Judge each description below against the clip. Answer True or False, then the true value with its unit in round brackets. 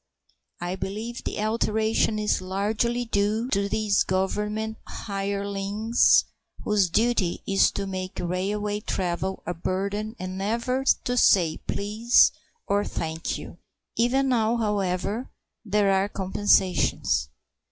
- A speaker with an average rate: False (120 wpm)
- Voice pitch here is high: True (205 Hz)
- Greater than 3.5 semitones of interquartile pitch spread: False (2.6 semitones)